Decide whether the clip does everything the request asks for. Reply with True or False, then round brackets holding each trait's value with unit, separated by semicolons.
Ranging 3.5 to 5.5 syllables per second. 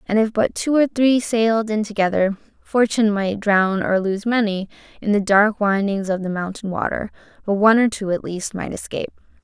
True (5.3 syllables/s)